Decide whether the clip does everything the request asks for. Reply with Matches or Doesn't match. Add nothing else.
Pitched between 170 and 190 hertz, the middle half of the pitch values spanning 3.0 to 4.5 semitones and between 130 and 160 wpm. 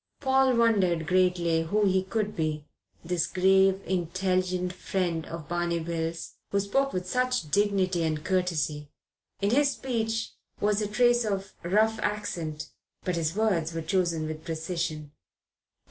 Matches